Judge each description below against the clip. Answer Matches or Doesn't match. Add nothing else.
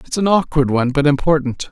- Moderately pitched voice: Matches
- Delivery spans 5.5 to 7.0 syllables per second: Matches